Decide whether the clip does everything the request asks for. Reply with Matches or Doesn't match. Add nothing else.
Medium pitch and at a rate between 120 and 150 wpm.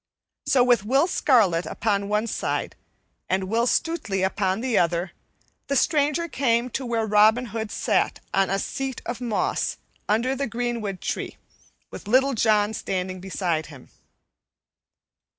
Doesn't match